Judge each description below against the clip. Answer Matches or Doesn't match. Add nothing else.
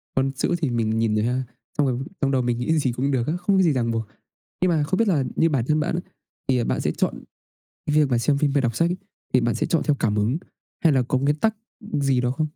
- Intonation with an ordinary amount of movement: Matches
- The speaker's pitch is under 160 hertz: Matches